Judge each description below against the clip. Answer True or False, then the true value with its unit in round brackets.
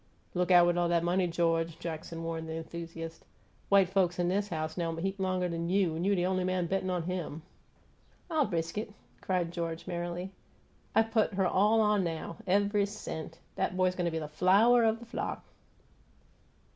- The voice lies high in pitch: False (180 Hz)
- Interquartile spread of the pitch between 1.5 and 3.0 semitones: True (2.6 semitones)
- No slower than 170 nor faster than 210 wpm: True (180 wpm)